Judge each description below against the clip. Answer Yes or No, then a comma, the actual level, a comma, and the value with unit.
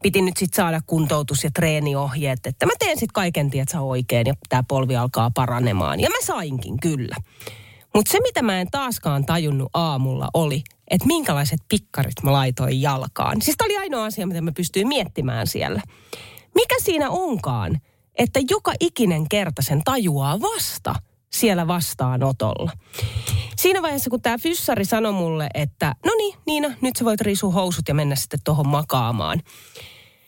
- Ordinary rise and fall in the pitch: No, wide, 8.2 semitones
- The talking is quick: Yes, fast, 160 wpm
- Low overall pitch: No, medium, 160 Hz